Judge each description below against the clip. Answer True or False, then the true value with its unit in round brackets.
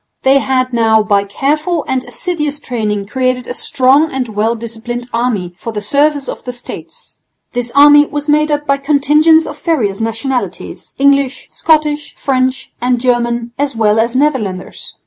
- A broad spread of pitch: False (4.0 semitones)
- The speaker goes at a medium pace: True (160 wpm)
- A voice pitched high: True (255 Hz)